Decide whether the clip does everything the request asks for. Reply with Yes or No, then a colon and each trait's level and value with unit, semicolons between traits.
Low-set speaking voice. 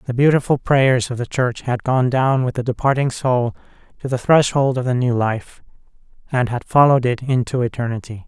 Yes: low, 125 Hz